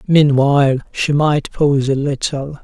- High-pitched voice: No, medium, 140 Hz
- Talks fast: No, slow, 135 wpm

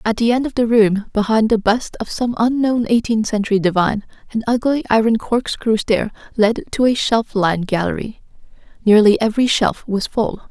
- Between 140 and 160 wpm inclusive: No, average, 175 wpm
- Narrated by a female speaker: Yes, female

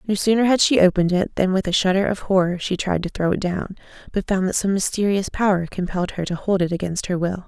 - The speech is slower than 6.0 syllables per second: No, 6.3 syllables/s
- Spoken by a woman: Yes, female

